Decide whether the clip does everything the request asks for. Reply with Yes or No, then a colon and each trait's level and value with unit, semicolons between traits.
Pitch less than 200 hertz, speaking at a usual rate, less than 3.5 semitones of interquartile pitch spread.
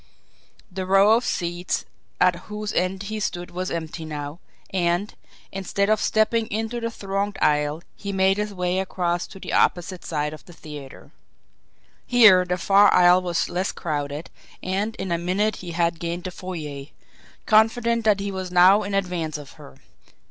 Yes: medium, 185 Hz; average, 170 wpm; average, 2.9 semitones